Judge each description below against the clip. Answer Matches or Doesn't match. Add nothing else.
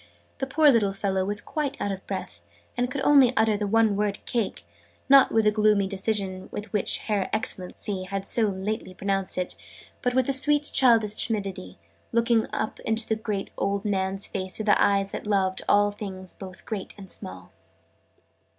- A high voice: Matches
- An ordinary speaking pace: Matches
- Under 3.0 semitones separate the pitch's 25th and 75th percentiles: Matches